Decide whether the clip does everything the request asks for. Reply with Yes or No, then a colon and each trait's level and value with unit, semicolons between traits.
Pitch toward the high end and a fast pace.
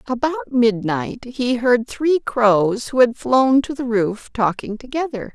No: high, 240 Hz; average, 155 wpm